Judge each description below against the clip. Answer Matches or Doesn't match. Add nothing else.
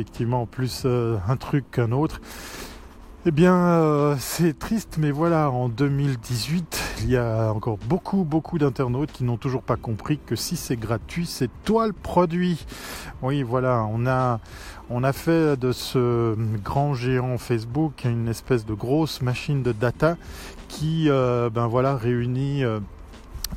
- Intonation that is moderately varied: Matches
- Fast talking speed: Doesn't match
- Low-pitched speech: Matches